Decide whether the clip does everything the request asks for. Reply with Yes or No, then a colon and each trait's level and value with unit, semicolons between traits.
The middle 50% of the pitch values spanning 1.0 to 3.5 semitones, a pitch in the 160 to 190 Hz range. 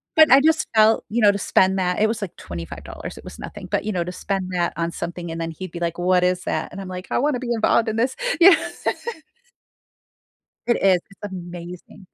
No: average, 3.9 semitones; medium, 185 Hz